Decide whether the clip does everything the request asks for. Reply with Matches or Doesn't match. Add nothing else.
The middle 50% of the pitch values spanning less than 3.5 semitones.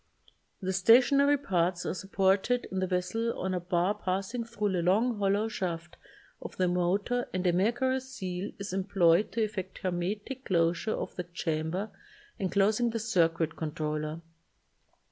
Doesn't match